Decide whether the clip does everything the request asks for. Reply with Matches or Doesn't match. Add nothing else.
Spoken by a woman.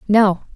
Matches